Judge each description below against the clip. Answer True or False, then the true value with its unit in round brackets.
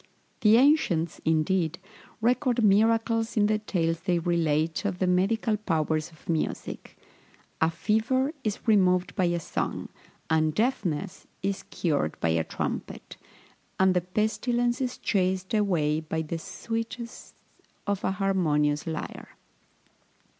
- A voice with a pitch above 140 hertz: True (185 Hz)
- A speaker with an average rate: False (125 wpm)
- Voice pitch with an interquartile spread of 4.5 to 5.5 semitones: True (5.2 semitones)